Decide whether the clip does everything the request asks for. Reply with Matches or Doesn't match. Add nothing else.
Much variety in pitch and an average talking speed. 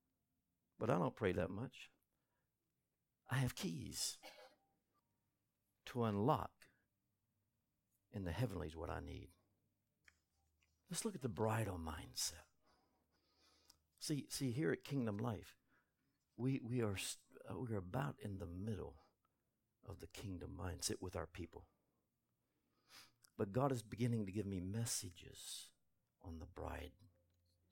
Doesn't match